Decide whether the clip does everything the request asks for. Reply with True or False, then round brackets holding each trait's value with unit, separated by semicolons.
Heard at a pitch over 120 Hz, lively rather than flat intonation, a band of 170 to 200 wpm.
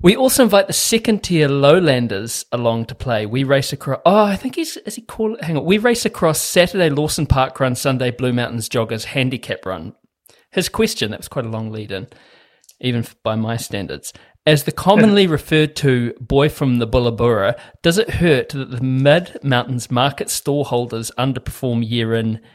True (135 Hz; 6.1 semitones; 185 wpm)